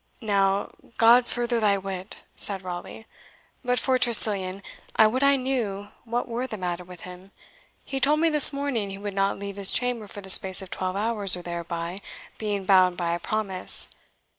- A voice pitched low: No, high, 200 Hz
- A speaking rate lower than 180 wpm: No, average, 185 wpm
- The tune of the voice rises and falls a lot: No, average, 4.1 semitones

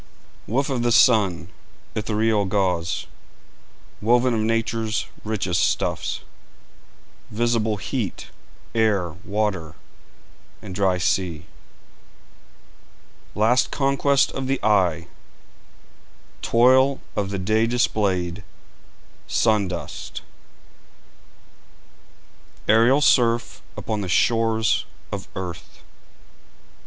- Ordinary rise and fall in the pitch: Yes, average, 3.7 semitones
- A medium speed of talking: No, slow, 85 wpm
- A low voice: Yes, low, 110 Hz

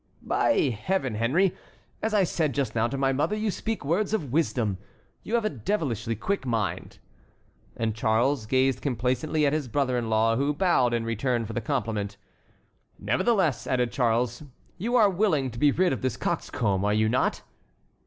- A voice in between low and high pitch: No, low, 130 Hz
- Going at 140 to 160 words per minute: No, average, 175 wpm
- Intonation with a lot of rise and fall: Yes, wide, 6.0 semitones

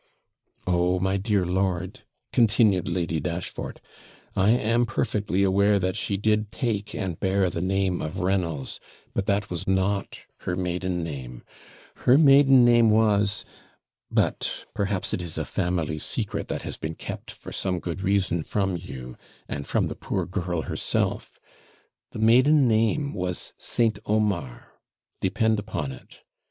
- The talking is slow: No, average, 145 wpm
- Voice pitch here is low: Yes, very low, 95 Hz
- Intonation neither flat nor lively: Yes, average, 3.3 semitones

